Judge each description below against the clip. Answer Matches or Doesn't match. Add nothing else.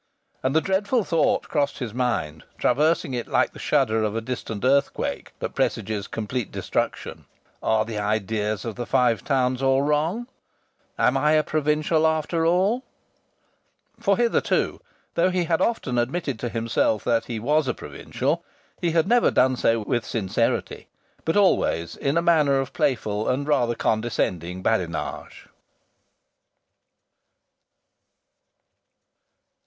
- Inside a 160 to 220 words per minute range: Doesn't match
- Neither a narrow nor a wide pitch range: Doesn't match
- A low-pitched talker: Matches